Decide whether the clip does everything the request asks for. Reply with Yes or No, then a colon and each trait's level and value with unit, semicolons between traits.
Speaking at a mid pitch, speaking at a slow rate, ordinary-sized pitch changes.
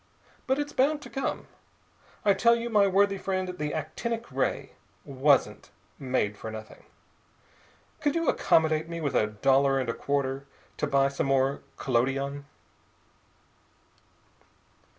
No: medium, 145 Hz; slow, 130 wpm; wide, 6.9 semitones